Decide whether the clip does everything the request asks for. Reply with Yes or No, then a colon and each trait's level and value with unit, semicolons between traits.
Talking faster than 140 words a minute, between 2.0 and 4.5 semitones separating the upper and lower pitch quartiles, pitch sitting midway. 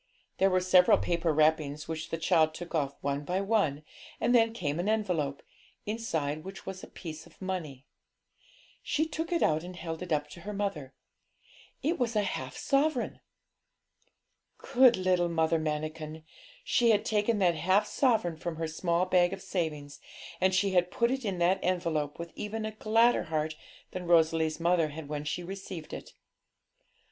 Yes: average, 175 wpm; average, 4.2 semitones; medium, 175 Hz